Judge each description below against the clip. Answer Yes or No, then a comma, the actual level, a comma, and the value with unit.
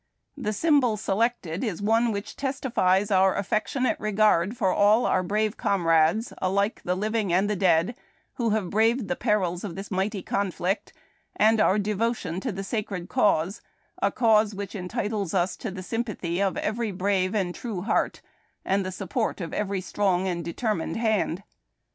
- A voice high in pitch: Yes, high, 200 Hz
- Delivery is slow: No, average, 170 wpm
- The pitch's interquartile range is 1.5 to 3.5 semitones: Yes, average, 2.9 semitones